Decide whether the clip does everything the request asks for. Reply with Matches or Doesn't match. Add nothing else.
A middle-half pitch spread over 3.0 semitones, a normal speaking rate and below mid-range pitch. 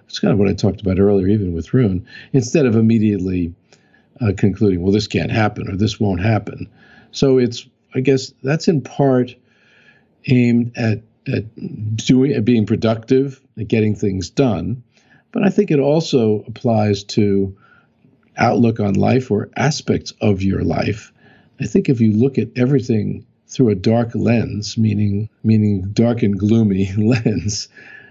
Matches